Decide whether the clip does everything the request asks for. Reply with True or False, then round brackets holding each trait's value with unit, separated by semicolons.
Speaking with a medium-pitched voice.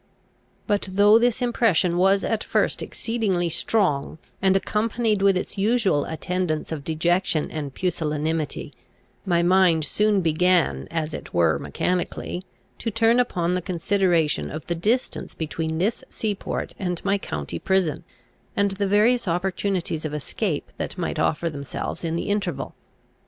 True (180 Hz)